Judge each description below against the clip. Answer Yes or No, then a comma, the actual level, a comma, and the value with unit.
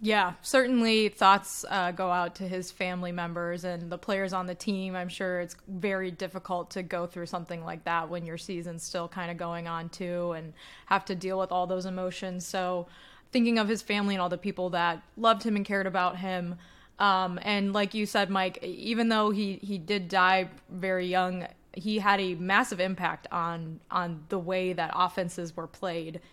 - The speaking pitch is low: No, medium, 185 Hz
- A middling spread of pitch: No, narrow, 1.9 semitones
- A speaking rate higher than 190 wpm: Yes, average, 200 wpm